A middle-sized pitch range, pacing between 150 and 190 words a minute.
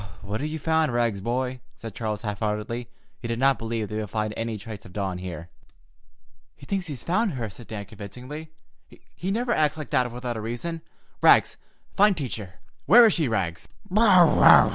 No: wide, 6.1 semitones; average, 185 wpm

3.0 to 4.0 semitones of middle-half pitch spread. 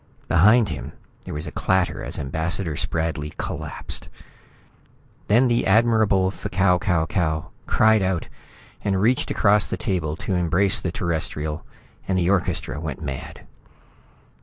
Yes: average, 3.7 semitones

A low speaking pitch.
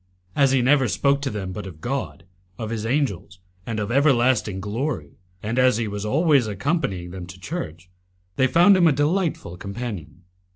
Yes: low, 120 Hz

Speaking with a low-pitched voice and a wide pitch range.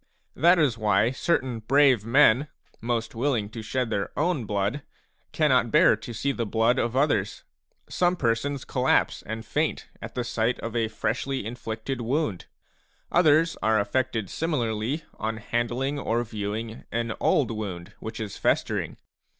No: low, 115 Hz; average, 3.7 semitones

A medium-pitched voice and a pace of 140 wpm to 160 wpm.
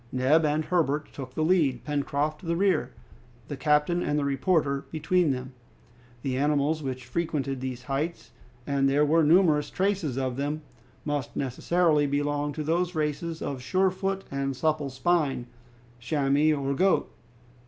Yes: medium, 150 Hz; average, 150 wpm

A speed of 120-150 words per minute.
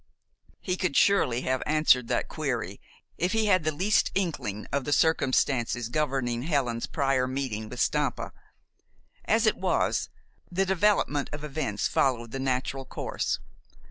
Yes: average, 140 wpm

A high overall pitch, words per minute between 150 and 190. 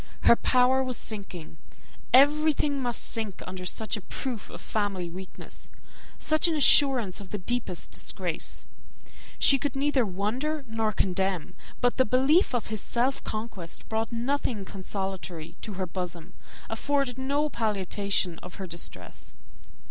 No: high, 220 Hz; average, 140 wpm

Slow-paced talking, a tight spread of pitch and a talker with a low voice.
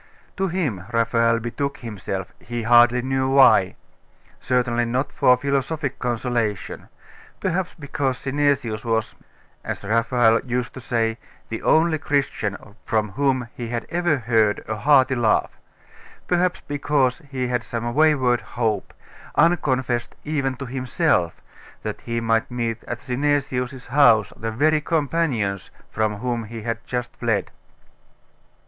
No: slow, 130 wpm; average, 3.5 semitones; low, 125 Hz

